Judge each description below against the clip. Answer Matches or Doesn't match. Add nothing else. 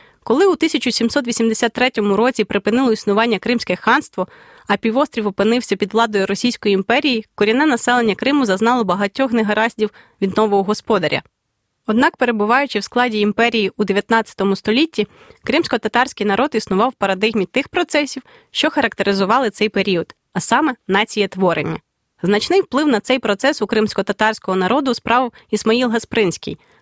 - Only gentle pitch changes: Doesn't match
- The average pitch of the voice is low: Doesn't match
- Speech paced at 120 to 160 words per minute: Matches